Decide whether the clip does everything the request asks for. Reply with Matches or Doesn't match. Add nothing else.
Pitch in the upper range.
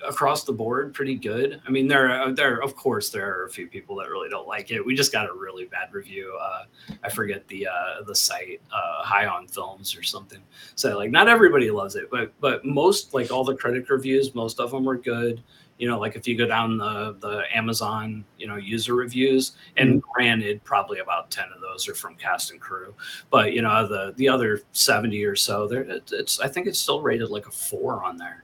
Doesn't match